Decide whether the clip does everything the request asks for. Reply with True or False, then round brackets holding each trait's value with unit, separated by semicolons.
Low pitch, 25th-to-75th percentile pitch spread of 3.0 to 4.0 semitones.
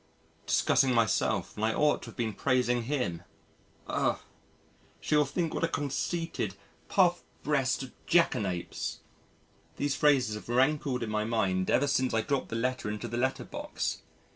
False (125 Hz; 4.4 semitones)